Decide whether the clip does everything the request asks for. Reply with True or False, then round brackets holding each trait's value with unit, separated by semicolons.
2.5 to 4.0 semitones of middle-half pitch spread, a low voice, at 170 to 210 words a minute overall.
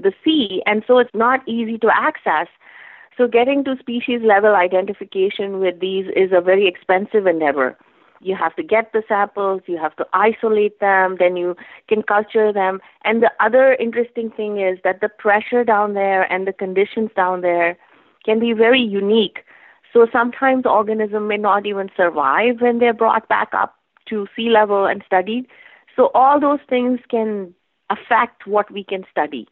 False (3.4 semitones; 210 Hz; 175 wpm)